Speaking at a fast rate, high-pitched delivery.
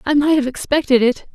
Yes: fast, 225 wpm; very high, 275 Hz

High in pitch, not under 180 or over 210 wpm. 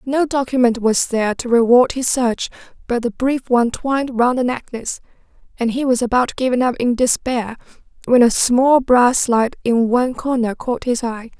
Yes: high, 245 Hz; average, 185 wpm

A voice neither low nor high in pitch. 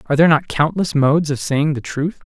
Yes: medium, 150 Hz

